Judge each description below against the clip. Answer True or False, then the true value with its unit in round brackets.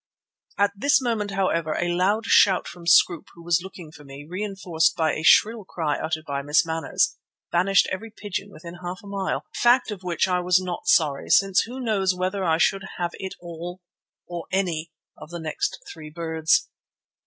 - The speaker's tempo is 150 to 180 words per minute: False (190 wpm)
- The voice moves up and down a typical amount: True (3.2 semitones)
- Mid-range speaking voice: True (180 Hz)